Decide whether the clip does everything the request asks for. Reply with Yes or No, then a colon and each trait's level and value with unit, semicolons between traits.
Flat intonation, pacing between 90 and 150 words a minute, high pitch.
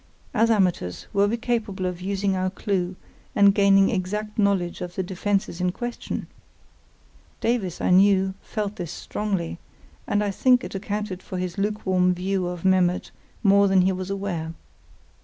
No: narrow, 2.0 semitones; average, 160 wpm; high, 195 Hz